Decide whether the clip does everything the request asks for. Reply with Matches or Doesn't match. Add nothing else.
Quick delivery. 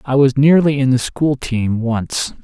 Doesn't match